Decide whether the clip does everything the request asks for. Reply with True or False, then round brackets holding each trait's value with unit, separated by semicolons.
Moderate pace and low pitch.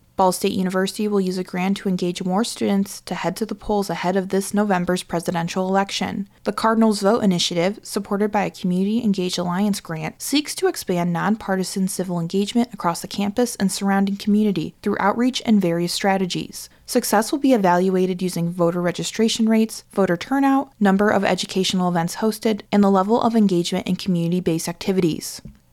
False (175 wpm; 195 Hz)